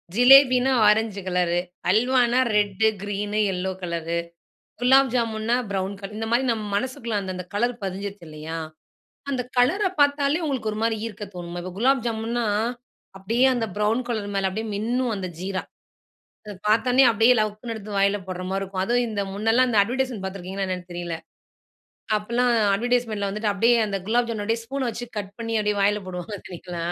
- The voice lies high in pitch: Yes, high, 215 Hz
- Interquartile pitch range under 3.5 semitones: No, average, 3.8 semitones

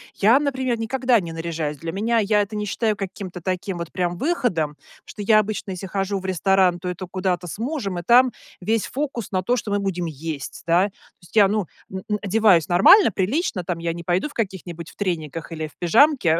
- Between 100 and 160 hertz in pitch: No, high, 190 Hz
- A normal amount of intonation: Yes, average, 4.1 semitones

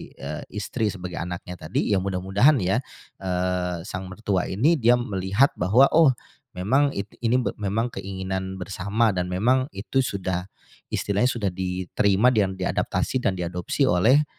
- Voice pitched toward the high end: No, very low, 95 Hz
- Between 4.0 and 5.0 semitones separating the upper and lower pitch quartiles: Yes, average, 4.3 semitones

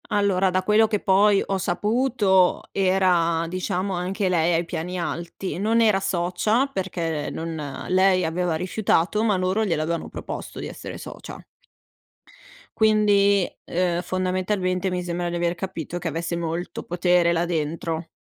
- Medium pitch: Yes, medium, 180 Hz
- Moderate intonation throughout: No, narrow, 2.3 semitones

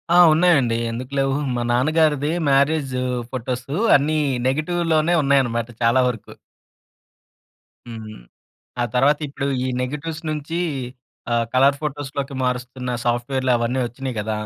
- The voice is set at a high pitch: No, low, 135 Hz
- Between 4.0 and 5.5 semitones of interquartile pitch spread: No, average, 3.3 semitones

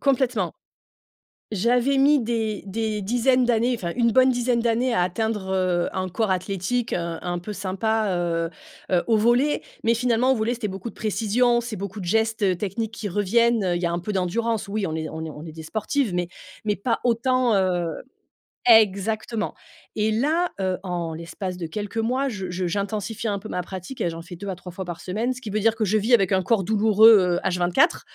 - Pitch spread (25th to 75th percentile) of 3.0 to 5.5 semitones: Yes, average, 4.2 semitones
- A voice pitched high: Yes, high, 210 Hz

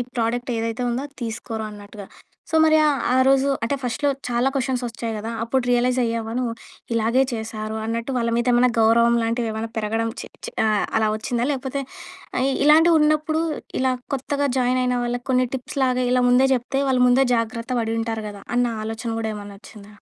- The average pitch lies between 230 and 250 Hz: Yes, high, 240 Hz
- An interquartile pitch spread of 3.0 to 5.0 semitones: No, narrow, 2.4 semitones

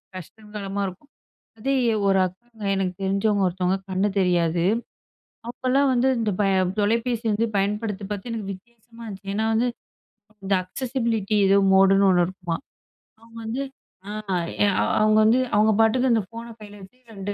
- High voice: Yes, high, 210 Hz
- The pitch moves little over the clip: No, average, 3.1 semitones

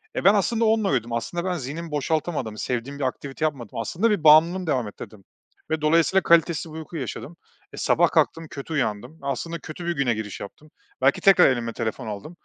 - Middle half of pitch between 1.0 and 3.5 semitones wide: No, average, 5.2 semitones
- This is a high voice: No, medium, 155 Hz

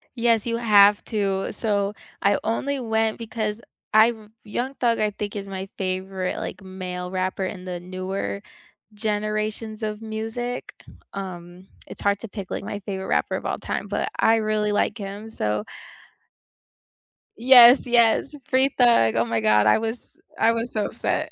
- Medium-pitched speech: No, high, 210 Hz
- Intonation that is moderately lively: Yes, average, 3.0 semitones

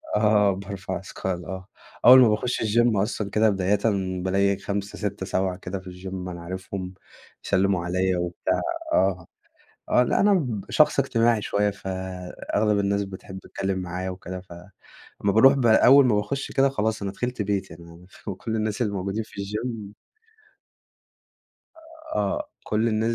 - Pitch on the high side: No, low, 100 Hz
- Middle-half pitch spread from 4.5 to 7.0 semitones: No, average, 2.9 semitones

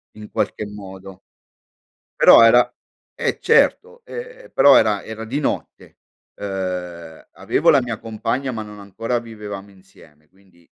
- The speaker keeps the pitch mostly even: No, average, 4.0 semitones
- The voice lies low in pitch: Yes, low, 105 Hz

